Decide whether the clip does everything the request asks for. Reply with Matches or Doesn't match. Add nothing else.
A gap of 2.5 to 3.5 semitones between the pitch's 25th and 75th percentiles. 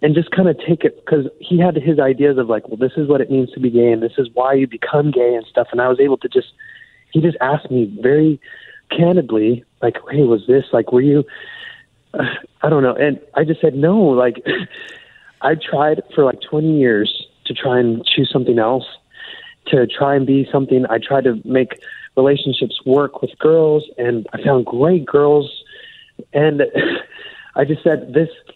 Doesn't match